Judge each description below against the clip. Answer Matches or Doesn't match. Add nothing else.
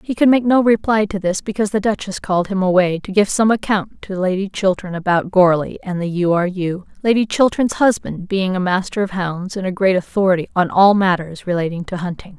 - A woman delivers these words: Matches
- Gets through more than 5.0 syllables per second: Matches